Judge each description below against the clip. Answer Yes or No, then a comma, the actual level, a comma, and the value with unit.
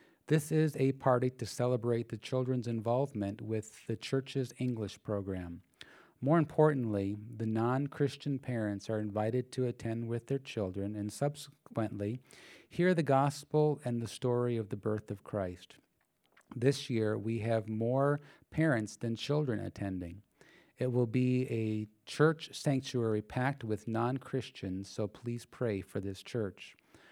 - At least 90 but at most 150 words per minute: Yes, average, 145 wpm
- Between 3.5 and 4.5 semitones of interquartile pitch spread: Yes, average, 3.9 semitones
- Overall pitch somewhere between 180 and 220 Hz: No, low, 120 Hz